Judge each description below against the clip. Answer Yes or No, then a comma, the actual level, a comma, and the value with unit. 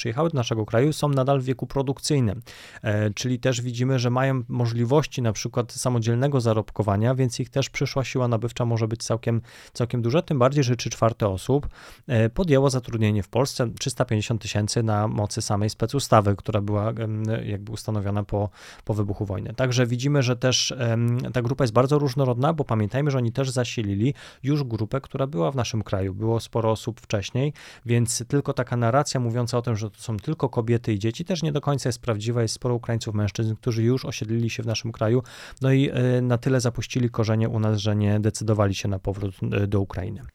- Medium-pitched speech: No, low, 120 Hz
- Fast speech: Yes, fast, 195 wpm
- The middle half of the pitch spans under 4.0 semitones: Yes, average, 3.1 semitones